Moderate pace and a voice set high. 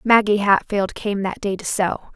Yes: average, 195 wpm; high, 200 Hz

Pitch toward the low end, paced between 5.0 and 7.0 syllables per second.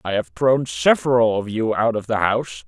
Yes: low, 115 Hz; 5.1 syllables/s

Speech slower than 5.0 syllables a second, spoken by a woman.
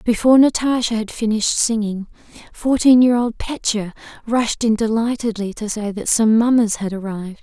No: 5.2 syllables/s; female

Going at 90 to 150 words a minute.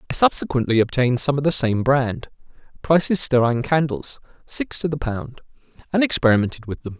Yes: average, 145 wpm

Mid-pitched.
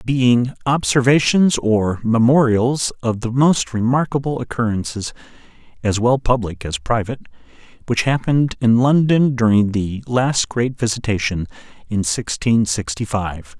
No: low, 120 Hz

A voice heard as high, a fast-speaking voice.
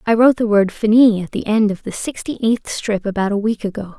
Yes: high, 215 Hz; fast, 255 wpm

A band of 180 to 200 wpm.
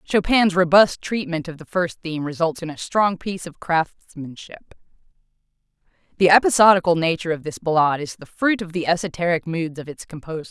No: average, 170 wpm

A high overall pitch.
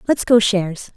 Yes: high, 205 Hz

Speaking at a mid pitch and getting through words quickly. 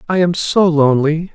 No: medium, 165 Hz; average, 180 wpm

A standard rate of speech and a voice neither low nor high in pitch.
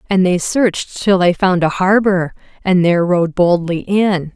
Yes: average, 180 wpm; medium, 180 Hz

